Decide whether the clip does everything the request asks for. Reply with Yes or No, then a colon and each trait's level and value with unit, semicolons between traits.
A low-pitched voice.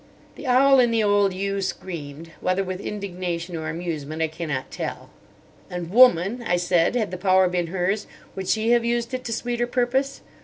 No: high, 190 Hz